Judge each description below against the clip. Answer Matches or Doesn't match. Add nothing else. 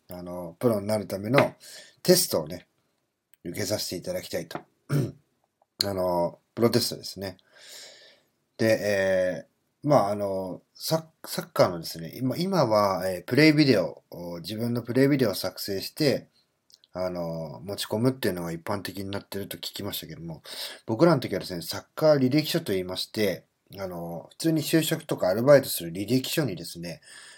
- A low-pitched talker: Matches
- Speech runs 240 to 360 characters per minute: Matches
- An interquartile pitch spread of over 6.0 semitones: Matches